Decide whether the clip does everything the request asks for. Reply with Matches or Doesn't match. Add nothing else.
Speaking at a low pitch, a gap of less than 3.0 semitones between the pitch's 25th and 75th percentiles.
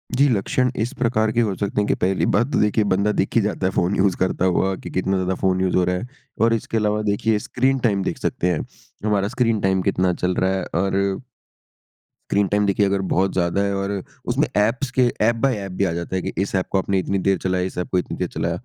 Matches